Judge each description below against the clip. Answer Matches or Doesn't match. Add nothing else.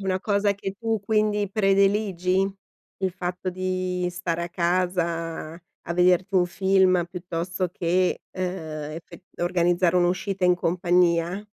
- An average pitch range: Doesn't match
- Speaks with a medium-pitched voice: Matches